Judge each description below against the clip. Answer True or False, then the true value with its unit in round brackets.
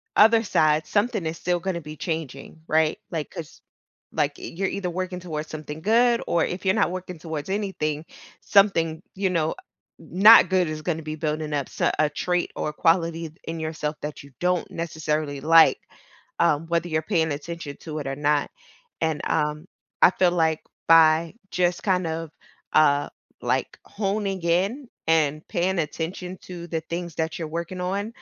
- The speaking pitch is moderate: True (165 Hz)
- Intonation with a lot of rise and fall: False (2.8 semitones)